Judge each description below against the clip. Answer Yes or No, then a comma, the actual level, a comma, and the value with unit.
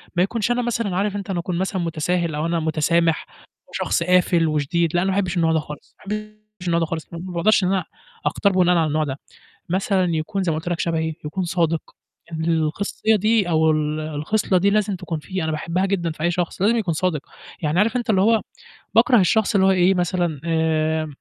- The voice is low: No, medium, 175 Hz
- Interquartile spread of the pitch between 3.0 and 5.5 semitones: Yes, average, 3.4 semitones